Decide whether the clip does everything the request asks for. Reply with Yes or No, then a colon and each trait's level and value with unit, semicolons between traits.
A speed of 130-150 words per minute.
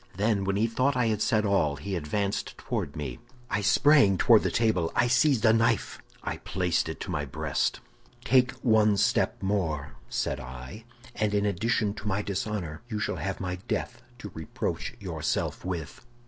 No: average, 175 wpm